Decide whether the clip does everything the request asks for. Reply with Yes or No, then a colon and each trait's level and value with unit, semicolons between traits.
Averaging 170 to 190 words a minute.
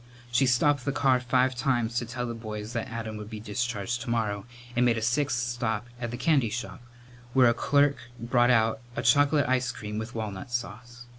No: average, 200 wpm